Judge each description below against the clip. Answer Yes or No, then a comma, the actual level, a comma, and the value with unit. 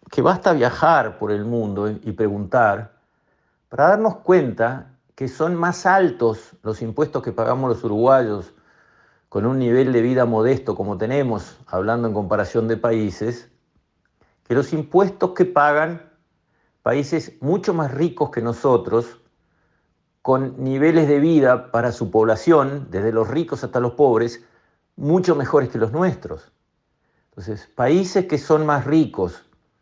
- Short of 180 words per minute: Yes, average, 140 wpm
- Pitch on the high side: No, low, 125 Hz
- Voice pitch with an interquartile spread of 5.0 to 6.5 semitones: Yes, wide, 5.4 semitones